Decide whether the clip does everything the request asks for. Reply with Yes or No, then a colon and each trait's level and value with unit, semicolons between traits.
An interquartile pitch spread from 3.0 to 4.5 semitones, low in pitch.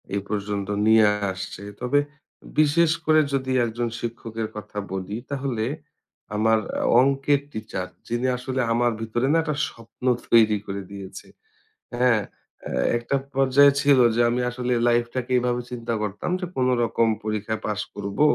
Yes: average, 3.3 semitones; low, 120 Hz